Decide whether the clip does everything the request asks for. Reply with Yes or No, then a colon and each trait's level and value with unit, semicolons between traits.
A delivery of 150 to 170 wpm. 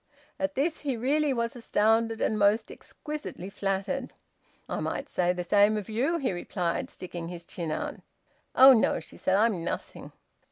Yes: average, 165 wpm